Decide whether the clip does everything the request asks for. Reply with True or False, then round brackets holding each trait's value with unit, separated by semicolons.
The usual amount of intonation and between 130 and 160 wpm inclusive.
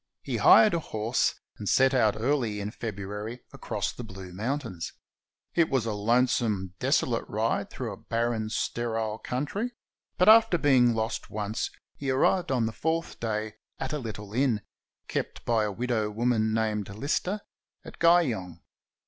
True (3.9 semitones; 155 wpm)